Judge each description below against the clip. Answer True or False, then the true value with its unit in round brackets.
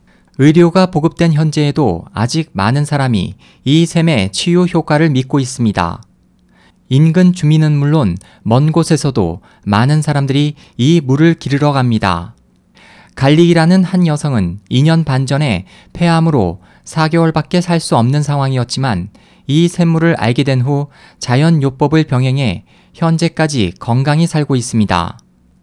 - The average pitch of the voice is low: False (145 Hz)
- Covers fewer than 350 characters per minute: True (275 characters per minute)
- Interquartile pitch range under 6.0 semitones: True (5.6 semitones)